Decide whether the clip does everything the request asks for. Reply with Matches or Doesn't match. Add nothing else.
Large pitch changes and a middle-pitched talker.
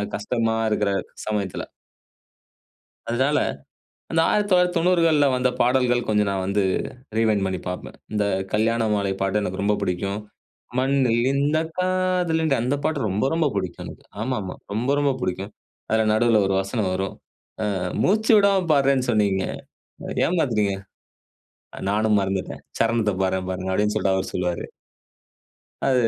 Doesn't match